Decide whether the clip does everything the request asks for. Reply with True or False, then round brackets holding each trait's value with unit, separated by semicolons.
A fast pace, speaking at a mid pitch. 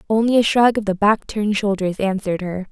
False (220 wpm; 205 Hz)